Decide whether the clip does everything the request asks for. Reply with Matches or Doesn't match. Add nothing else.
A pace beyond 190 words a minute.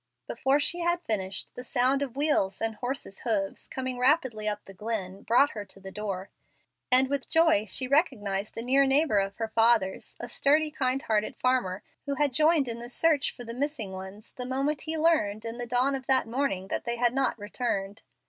Matches